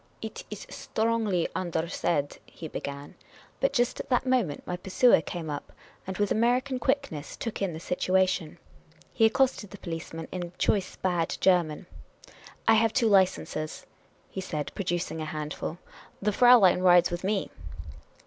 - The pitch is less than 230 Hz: Yes, medium, 185 Hz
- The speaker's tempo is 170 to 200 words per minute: Yes, average, 175 wpm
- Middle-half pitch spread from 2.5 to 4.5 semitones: No, average, 5.2 semitones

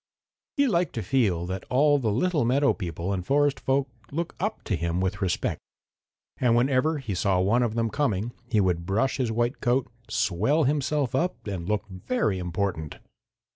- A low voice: Yes, low, 115 Hz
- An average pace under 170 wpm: No, average, 175 wpm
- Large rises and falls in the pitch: Yes, wide, 6.6 semitones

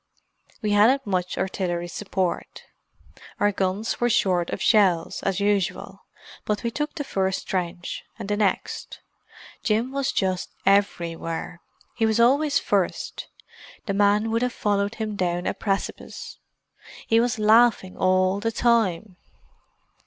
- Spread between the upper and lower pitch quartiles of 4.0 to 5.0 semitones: No, average, 3.3 semitones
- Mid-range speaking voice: No, high, 205 Hz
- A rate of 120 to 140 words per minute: Yes, slow, 135 wpm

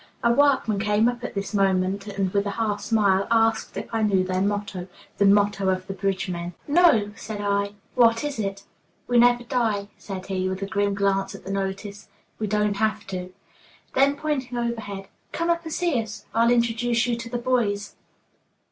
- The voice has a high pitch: Yes, high, 205 Hz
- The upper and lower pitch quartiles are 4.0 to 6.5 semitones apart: No, average, 3.1 semitones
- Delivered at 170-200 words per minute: Yes, average, 190 wpm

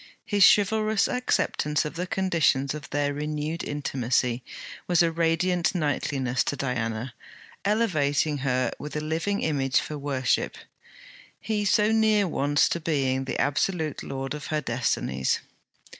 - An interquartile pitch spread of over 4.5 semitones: Yes, average, 4.9 semitones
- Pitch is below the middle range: No, medium, 150 Hz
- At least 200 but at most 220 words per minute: No, slow, 135 wpm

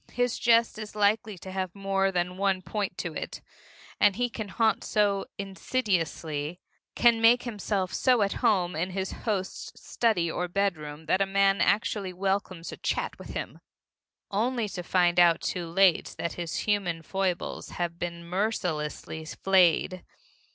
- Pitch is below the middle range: No, high, 195 Hz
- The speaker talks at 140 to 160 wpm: Yes, average, 155 wpm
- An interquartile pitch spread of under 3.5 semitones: Yes, average, 3.1 semitones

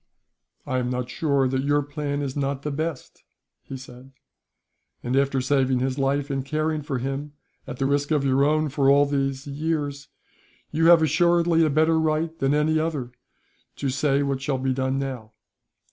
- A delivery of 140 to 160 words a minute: No, average, 180 wpm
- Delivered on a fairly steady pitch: Yes, narrow, 2.3 semitones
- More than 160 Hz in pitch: No, medium, 140 Hz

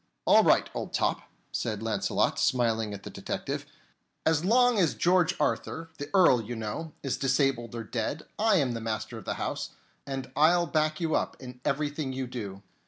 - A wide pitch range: Yes, wide, 5.8 semitones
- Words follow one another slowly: No, average, 180 wpm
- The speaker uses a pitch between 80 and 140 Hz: Yes, low, 135 Hz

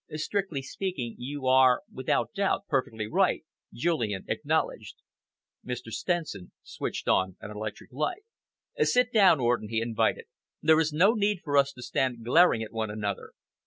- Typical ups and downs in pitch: No, wide, 7.0 semitones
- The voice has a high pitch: No, low, 130 Hz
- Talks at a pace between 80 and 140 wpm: No, average, 150 wpm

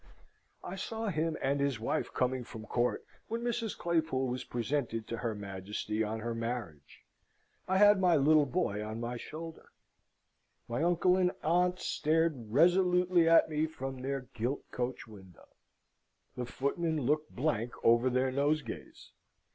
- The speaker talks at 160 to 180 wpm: No, average, 145 wpm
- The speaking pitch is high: No, medium, 140 Hz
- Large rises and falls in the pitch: Yes, wide, 6.0 semitones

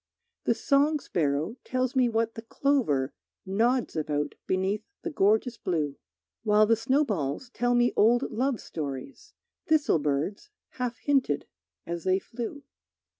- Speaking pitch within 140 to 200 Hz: No, high, 225 Hz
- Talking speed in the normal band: No, slow, 130 wpm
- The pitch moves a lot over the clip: Yes, wide, 7.1 semitones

